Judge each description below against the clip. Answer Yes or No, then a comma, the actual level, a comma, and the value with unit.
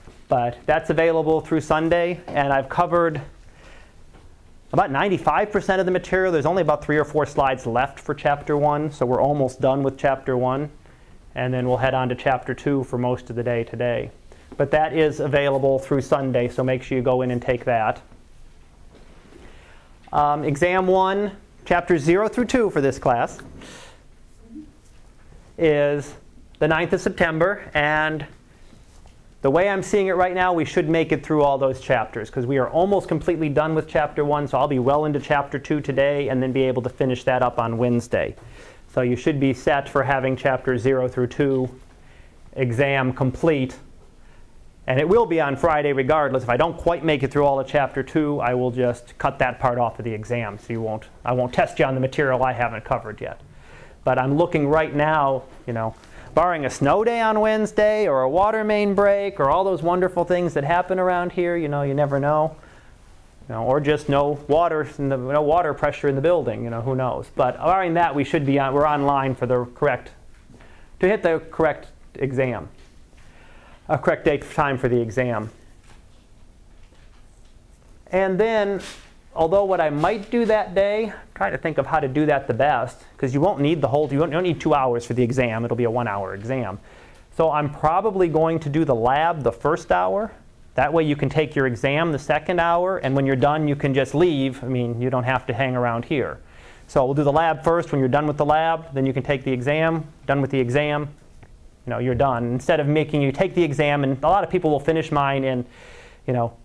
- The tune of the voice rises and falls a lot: No, average, 4.0 semitones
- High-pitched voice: No, medium, 140 Hz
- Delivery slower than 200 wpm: No, fast, 205 wpm